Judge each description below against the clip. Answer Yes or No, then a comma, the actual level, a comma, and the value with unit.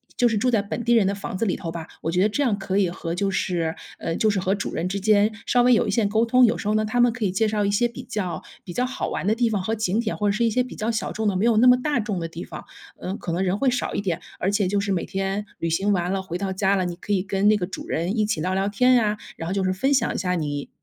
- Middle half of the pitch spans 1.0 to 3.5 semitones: Yes, average, 3.1 semitones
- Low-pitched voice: No, high, 200 Hz